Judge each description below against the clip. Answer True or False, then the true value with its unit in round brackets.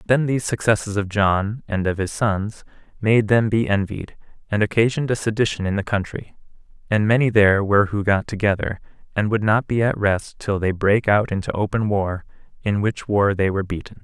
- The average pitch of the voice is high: False (105 Hz)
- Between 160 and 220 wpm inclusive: True (200 wpm)